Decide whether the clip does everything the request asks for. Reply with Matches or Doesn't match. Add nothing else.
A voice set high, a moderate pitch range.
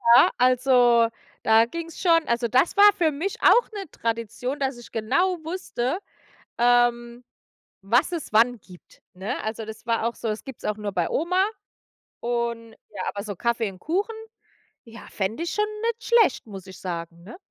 Doesn't match